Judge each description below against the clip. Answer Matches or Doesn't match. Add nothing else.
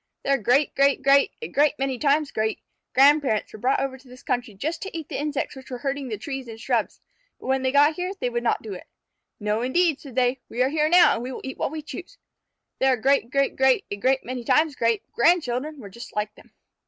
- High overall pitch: Matches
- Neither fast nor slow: Doesn't match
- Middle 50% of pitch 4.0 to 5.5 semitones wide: Doesn't match